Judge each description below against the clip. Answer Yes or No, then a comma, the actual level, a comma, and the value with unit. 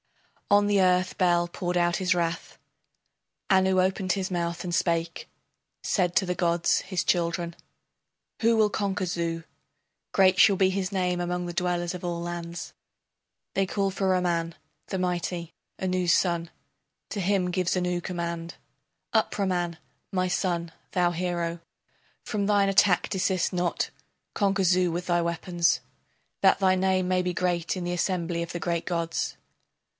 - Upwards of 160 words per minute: No, average, 155 wpm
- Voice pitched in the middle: Yes, medium, 180 Hz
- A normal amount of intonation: No, narrow, 1.6 semitones